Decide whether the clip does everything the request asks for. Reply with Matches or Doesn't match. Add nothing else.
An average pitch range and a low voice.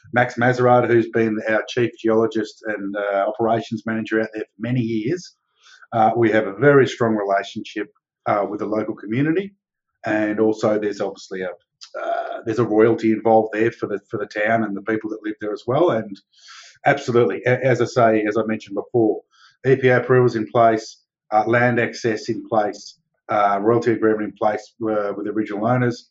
Doesn't match